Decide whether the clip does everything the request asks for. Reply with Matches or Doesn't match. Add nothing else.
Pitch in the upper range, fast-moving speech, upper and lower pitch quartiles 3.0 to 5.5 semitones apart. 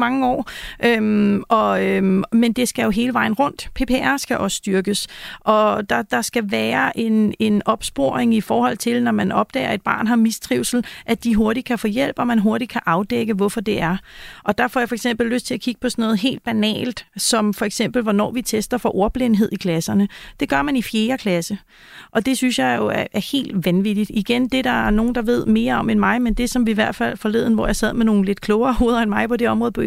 Doesn't match